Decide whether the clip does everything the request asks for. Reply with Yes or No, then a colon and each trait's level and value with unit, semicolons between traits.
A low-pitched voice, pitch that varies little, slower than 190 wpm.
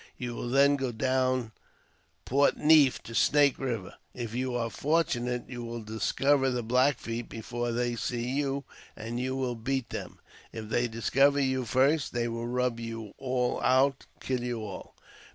Yes: low, 125 Hz; narrow, 2.3 semitones; average, 170 wpm